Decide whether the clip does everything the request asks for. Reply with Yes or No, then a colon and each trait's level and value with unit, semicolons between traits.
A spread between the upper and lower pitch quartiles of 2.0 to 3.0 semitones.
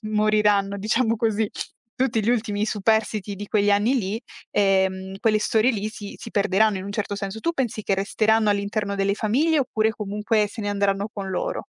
No: narrow, 1.6 semitones